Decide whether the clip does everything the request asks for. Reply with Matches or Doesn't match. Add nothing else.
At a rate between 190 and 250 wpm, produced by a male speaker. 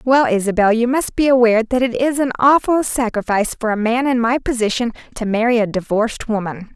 Doesn't match